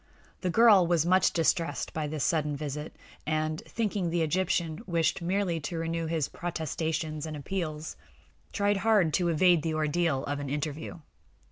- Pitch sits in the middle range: Yes, medium, 165 Hz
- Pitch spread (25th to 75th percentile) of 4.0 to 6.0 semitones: No, narrow, 2.4 semitones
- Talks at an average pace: Yes, average, 160 wpm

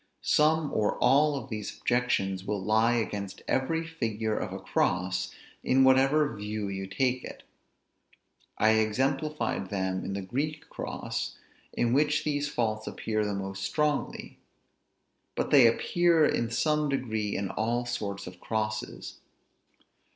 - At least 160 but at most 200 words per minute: No, slow, 135 wpm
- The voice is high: No, low, 115 Hz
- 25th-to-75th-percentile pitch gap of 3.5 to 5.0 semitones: No, wide, 5.5 semitones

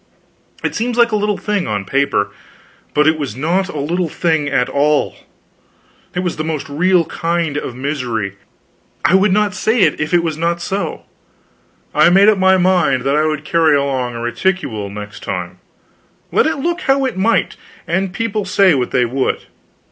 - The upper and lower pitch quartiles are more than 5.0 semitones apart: Yes, wide, 5.5 semitones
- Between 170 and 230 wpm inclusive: Yes, average, 185 wpm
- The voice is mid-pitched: Yes, medium, 165 Hz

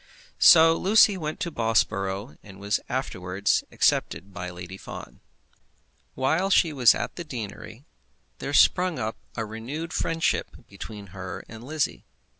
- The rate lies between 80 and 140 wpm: Yes, slow, 135 wpm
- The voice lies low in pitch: Yes, low, 115 Hz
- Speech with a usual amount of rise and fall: No, wide, 8.2 semitones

